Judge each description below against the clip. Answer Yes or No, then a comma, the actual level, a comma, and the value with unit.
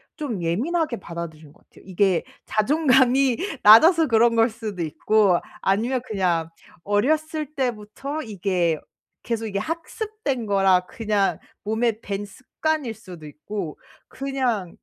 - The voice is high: Yes, high, 220 Hz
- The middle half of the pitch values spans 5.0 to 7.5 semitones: Yes, wide, 5.6 semitones